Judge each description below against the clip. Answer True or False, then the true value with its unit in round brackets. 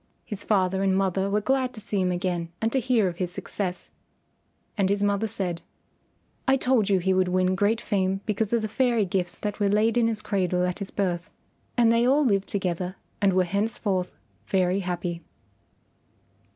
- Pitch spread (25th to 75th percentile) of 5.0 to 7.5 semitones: False (3.0 semitones)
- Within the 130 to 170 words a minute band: False (190 wpm)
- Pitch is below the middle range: False (195 Hz)